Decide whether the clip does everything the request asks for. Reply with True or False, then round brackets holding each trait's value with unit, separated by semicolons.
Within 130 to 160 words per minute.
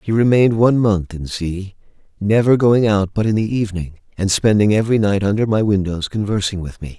False (200 wpm)